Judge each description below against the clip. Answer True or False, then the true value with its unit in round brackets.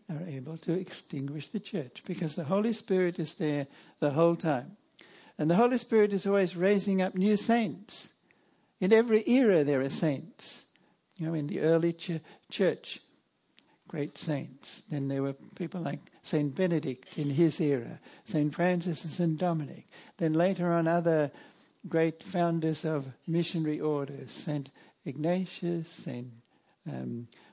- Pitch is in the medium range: True (170 Hz)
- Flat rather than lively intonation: False (3.8 semitones)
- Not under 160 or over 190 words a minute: False (145 wpm)